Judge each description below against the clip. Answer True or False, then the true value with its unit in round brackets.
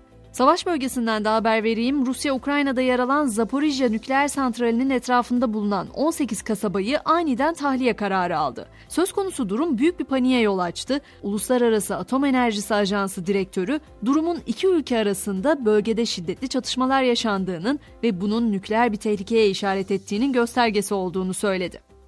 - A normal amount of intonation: True (4.7 semitones)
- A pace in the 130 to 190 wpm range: True (135 wpm)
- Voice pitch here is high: True (235 Hz)